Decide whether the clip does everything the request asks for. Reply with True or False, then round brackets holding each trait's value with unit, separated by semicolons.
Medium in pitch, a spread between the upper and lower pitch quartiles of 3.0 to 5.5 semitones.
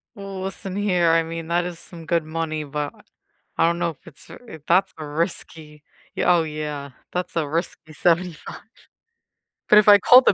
False (165 Hz; 2.5 semitones)